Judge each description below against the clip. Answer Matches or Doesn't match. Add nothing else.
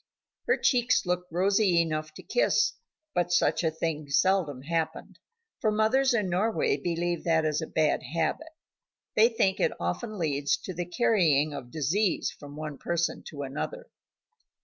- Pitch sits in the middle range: Matches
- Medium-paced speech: Matches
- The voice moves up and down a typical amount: Matches